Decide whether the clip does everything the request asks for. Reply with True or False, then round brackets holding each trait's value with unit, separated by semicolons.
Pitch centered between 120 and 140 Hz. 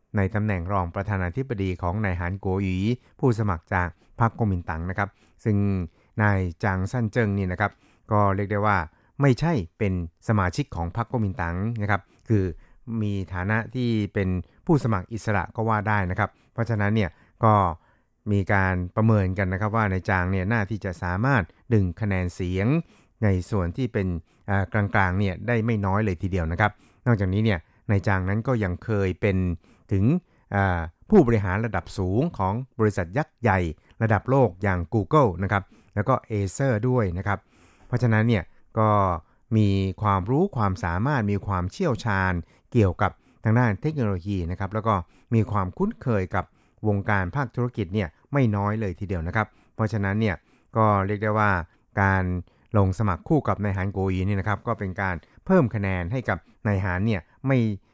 False (105 Hz)